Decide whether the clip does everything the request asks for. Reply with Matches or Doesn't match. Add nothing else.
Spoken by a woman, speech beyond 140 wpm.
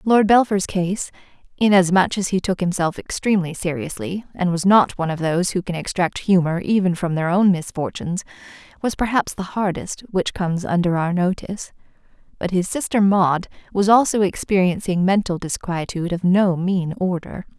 Matches